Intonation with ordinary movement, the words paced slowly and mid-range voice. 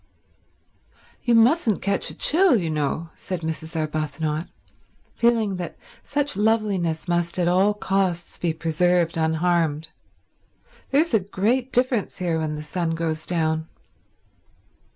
Yes: average, 4.7 semitones; slow, 125 wpm; medium, 175 Hz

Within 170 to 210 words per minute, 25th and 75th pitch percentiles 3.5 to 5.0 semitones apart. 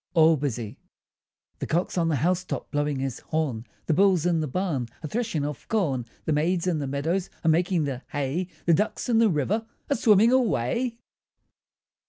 Yes: average, 185 wpm; average, 4.7 semitones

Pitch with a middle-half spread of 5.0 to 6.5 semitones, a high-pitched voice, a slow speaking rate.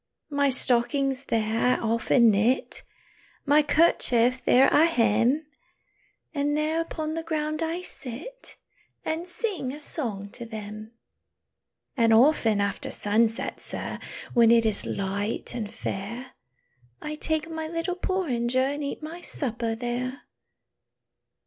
Yes: average, 5.3 semitones; very high, 255 Hz; slow, 125 wpm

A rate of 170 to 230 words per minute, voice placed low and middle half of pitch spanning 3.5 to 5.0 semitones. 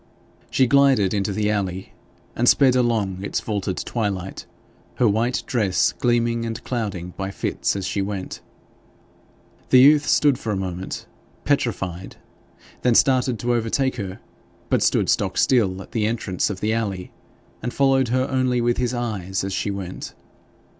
No: average, 155 wpm; low, 110 Hz; average, 4.2 semitones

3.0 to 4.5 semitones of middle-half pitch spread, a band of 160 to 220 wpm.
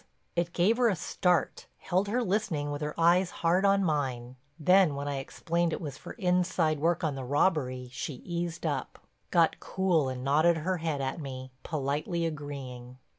Yes: average, 4.1 semitones; average, 170 wpm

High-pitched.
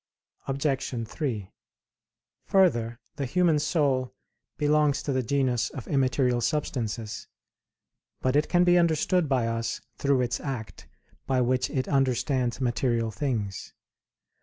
No: low, 130 Hz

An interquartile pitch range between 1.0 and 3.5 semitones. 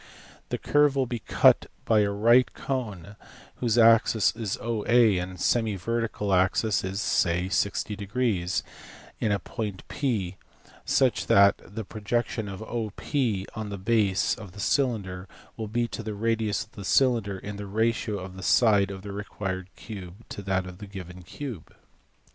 Yes: average, 3.0 semitones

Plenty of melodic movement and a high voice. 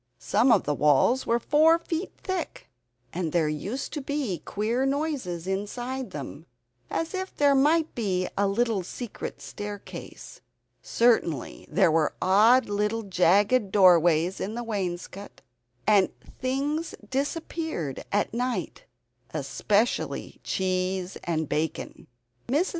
Yes: wide, 6.4 semitones; high, 210 Hz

